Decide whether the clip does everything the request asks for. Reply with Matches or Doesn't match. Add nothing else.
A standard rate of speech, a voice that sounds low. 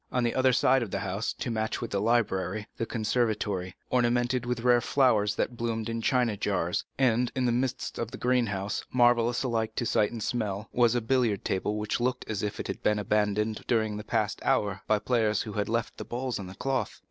Doesn't match